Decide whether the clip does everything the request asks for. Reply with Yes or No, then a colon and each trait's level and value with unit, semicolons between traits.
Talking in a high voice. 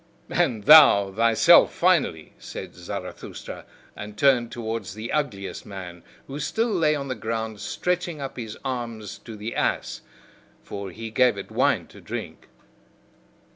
No: low, 115 Hz